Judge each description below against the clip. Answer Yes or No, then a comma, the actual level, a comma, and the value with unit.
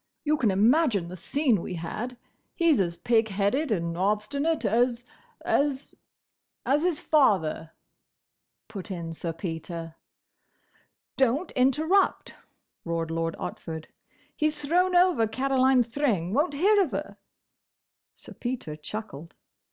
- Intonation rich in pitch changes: Yes, wide, 9.0 semitones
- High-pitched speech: Yes, high, 235 Hz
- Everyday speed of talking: No, slow, 115 wpm